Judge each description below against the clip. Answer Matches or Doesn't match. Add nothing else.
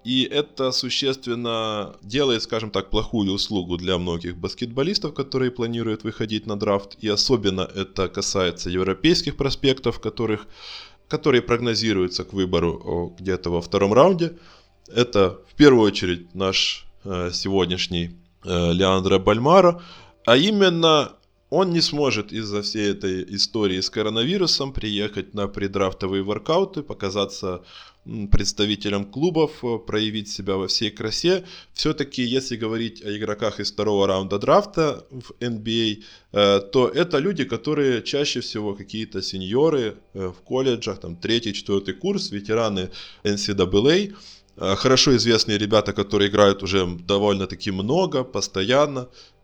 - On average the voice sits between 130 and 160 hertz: Doesn't match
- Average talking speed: Matches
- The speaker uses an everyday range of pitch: Matches